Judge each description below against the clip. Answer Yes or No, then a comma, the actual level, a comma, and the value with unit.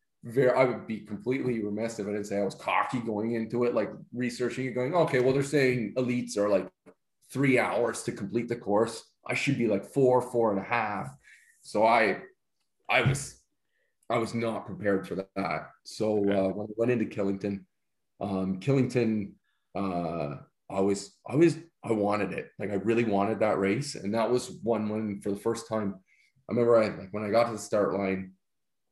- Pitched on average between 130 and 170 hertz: No, low, 110 Hz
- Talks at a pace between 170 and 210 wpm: Yes, average, 195 wpm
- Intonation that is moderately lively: Yes, average, 3.4 semitones